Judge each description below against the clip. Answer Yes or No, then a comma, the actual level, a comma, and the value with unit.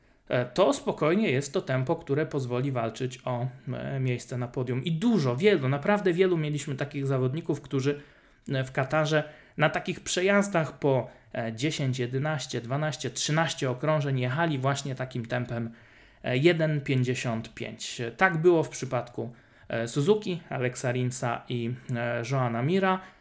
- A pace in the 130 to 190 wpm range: No, average, 120 wpm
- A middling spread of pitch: Yes, average, 3.9 semitones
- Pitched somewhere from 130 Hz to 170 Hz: Yes, low, 135 Hz